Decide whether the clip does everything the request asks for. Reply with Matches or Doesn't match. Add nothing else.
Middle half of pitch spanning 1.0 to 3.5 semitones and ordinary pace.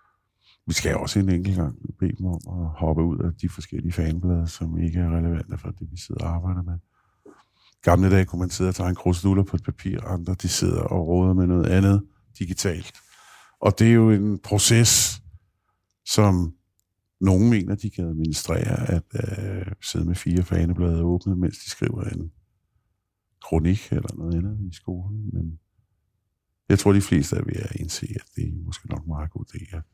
Matches